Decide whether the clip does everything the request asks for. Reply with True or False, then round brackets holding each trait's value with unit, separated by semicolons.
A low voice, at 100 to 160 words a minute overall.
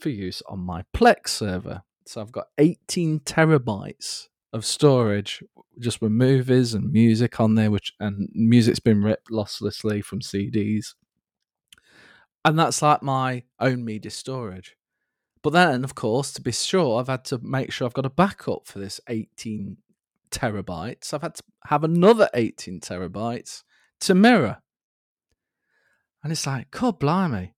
True (120 Hz; 150 wpm)